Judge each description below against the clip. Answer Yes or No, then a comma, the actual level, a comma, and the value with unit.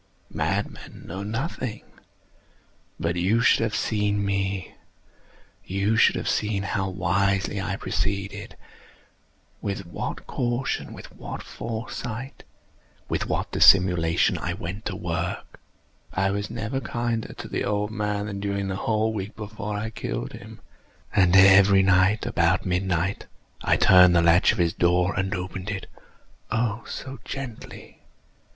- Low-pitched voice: Yes, low, 100 Hz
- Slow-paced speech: Yes, slow, 130 wpm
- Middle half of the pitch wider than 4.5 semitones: No, narrow, 2.6 semitones